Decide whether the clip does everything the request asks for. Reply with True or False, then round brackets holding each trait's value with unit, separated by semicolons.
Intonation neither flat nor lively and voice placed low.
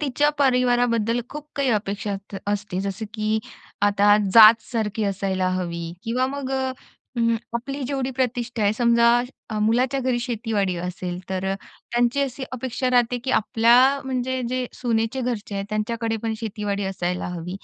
False (3.7 semitones; 230 Hz)